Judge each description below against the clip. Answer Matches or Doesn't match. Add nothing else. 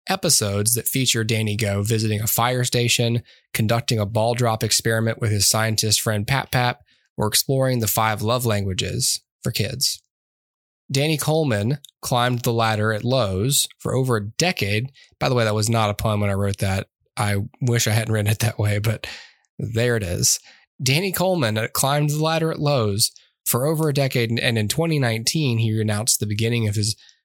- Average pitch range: Matches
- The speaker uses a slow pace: Doesn't match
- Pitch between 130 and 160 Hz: Doesn't match